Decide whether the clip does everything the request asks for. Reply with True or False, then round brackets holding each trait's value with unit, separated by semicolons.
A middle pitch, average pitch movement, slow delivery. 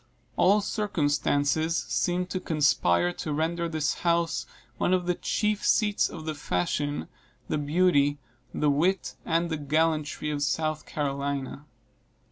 True (155 Hz; 3.1 semitones; 130 wpm)